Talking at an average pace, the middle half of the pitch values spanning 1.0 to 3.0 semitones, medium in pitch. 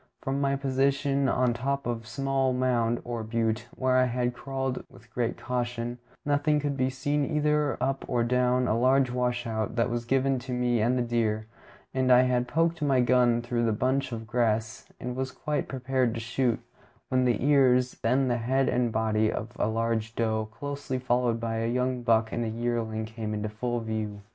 No: average, 190 wpm; narrow, 2.4 semitones; low, 125 Hz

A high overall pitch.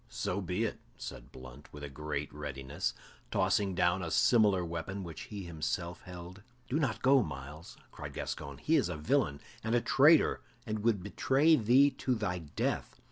No: very low, 90 Hz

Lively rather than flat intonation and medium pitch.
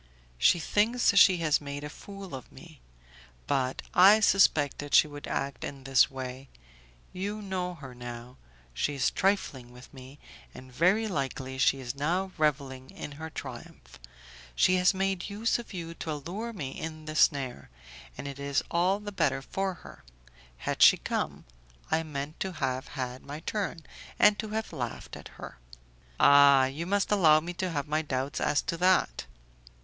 Yes: wide, 5.7 semitones; medium, 150 Hz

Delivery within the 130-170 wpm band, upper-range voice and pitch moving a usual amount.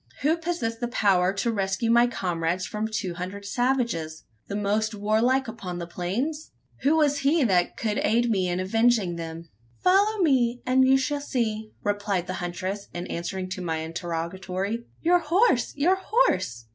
No: average, 165 wpm; high, 215 Hz; wide, 6.0 semitones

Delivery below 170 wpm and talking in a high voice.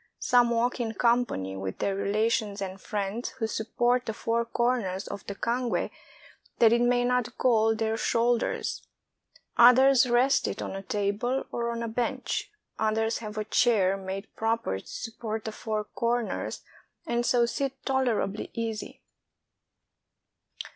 Yes: average, 145 wpm; high, 230 Hz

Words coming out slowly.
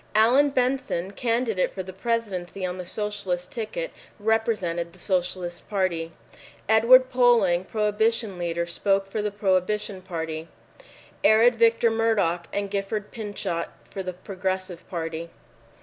Yes: slow, 125 wpm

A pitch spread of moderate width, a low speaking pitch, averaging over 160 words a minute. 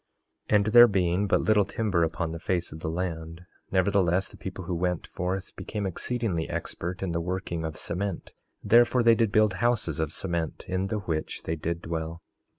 Yes: average, 3.4 semitones; very low, 90 Hz; average, 190 wpm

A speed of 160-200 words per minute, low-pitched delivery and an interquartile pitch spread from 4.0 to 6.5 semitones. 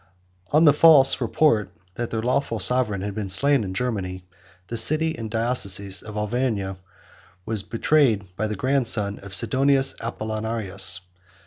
No: average, 145 wpm; low, 110 Hz; average, 4.5 semitones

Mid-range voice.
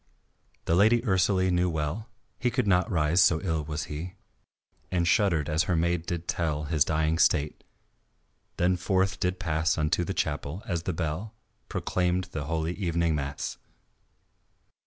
No: very low, 85 Hz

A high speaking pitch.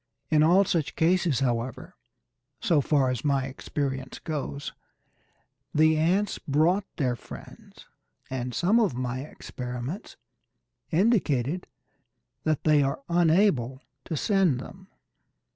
No: medium, 150 Hz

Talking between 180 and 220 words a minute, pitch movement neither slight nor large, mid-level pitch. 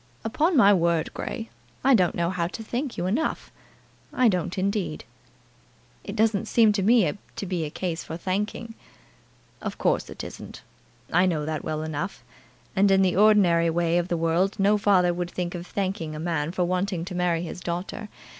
Yes: average, 185 wpm; average, 3.2 semitones; medium, 180 Hz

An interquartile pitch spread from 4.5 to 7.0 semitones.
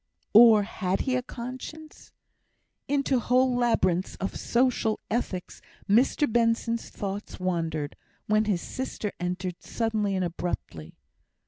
Yes: average, 5.0 semitones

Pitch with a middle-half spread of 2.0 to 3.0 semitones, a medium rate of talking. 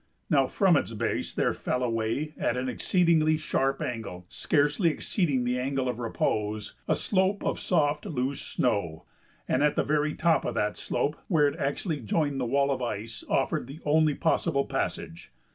No: average, 3.9 semitones; average, 170 wpm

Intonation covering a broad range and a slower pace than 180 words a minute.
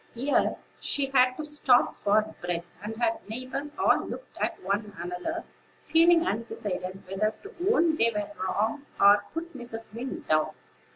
Yes: wide, 6.1 semitones; average, 160 wpm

